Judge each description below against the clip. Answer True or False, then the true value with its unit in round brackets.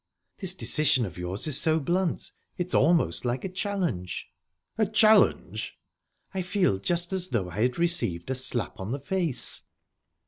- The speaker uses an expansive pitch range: True (7.5 semitones)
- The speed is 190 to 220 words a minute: False (160 wpm)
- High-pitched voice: False (160 Hz)